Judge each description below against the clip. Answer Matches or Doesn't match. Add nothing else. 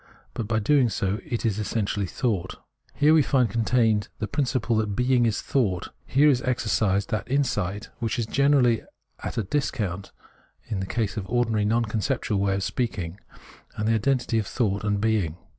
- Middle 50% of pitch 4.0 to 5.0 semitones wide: Doesn't match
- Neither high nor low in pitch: Doesn't match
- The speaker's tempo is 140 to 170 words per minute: Doesn't match